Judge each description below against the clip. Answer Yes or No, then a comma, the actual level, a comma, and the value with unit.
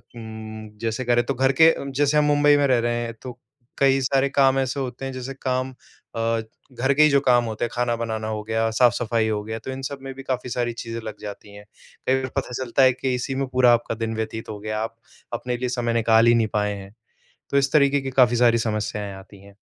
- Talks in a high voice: No, low, 120 Hz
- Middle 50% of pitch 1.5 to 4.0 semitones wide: Yes, average, 3.0 semitones